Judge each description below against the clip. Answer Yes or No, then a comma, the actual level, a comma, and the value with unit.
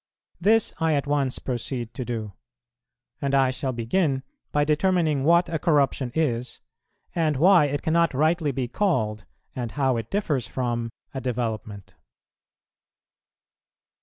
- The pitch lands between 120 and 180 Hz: Yes, low, 135 Hz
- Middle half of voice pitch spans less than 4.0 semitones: No, average, 4.7 semitones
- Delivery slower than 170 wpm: Yes, slow, 135 wpm